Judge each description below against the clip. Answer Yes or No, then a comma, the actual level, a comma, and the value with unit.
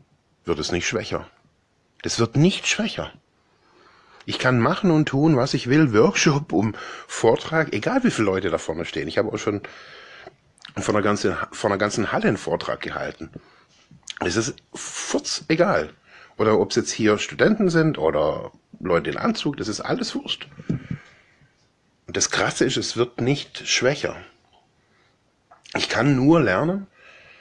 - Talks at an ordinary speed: Yes, average, 155 wpm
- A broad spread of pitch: Yes, wide, 7.3 semitones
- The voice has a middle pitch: Yes, medium, 150 Hz